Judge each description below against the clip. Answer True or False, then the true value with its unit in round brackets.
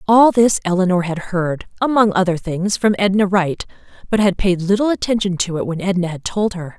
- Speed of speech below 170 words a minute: False (205 wpm)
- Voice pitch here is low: False (190 Hz)